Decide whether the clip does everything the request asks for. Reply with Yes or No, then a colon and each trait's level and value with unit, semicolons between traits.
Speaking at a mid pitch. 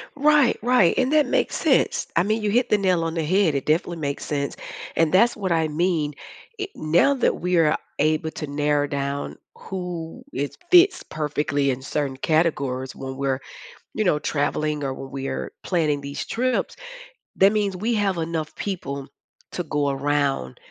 Yes: medium, 160 Hz